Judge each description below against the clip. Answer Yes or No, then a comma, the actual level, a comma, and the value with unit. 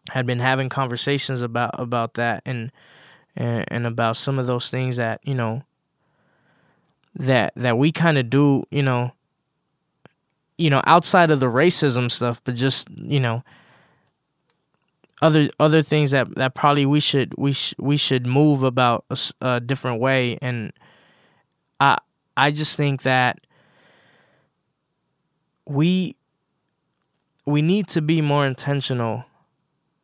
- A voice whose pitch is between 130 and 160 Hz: Yes, low, 135 Hz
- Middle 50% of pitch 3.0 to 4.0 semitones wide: Yes, average, 3.7 semitones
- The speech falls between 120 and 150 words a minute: Yes, slow, 135 wpm